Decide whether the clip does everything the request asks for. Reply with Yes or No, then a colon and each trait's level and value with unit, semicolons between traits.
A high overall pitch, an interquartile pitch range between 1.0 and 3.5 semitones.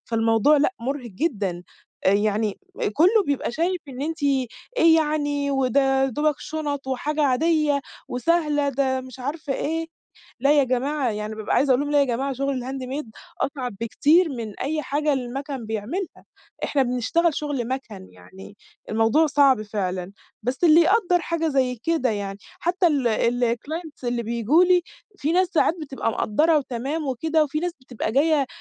No: very high, 275 Hz; average, 4.3 semitones